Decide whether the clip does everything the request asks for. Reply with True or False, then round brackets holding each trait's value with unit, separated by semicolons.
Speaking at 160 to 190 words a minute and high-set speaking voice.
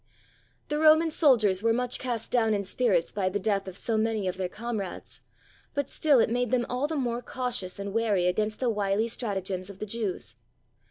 False (200 wpm; 220 Hz)